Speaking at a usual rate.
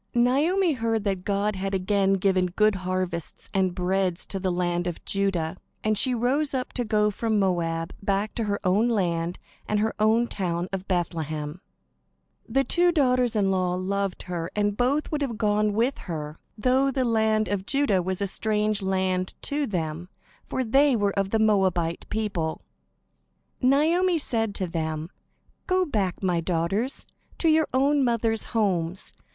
Yes: average, 165 wpm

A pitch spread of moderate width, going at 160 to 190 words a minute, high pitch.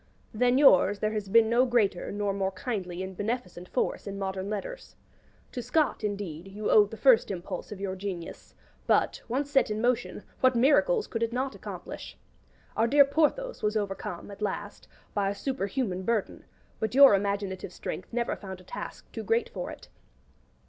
Yes: average, 4.3 semitones; average, 175 wpm; high, 210 Hz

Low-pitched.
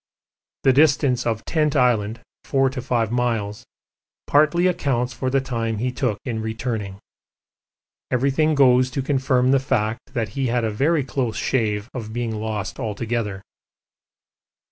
Yes: low, 125 Hz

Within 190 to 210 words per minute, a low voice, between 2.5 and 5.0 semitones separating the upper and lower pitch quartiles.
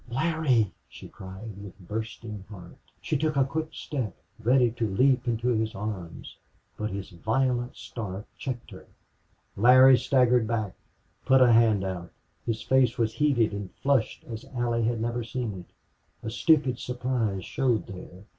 No: average, 155 wpm; low, 115 Hz; average, 3.6 semitones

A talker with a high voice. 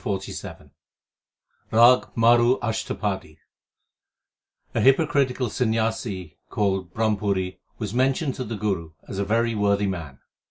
No: low, 110 Hz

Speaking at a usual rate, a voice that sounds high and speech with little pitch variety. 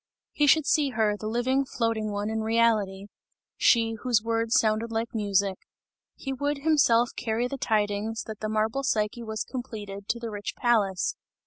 Yes: average, 165 wpm; high, 225 Hz; narrow, 2.2 semitones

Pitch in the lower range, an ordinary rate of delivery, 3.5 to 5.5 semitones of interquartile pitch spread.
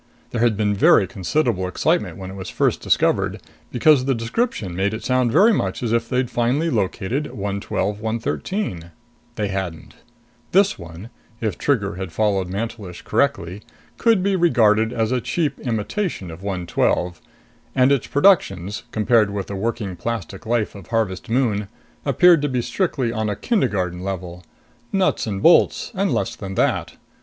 Yes: low, 110 Hz; average, 160 wpm; average, 4.9 semitones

